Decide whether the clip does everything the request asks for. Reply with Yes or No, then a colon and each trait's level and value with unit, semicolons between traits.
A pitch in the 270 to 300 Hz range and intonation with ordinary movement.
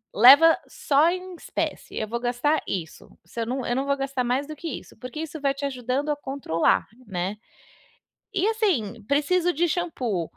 Yes: very high, 275 Hz; average, 4.6 semitones